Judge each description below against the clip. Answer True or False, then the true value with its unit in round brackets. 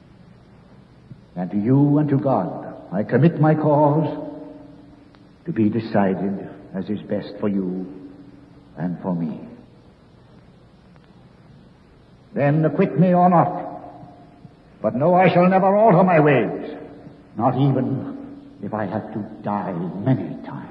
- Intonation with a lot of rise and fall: True (6.9 semitones)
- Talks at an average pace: False (125 wpm)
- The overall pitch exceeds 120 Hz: True (140 Hz)